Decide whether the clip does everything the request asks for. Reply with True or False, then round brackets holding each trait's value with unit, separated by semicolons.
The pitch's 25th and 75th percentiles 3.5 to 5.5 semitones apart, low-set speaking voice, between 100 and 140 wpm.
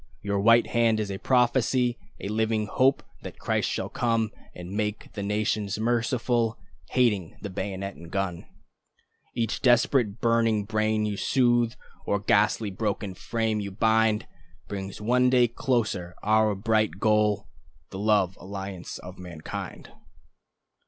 False (2.7 semitones; 110 Hz; 135 wpm)